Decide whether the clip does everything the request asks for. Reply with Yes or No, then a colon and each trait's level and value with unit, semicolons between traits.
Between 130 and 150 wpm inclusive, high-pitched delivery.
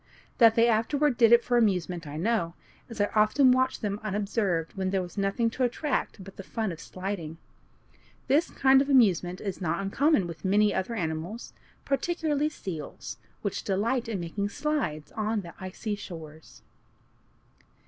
No: average, 160 wpm; high, 205 Hz